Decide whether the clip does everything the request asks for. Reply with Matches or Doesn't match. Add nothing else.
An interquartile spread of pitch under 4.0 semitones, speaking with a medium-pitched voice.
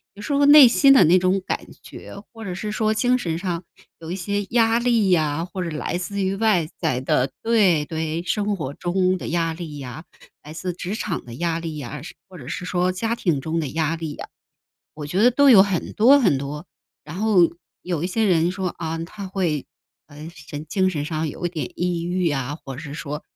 Doesn't match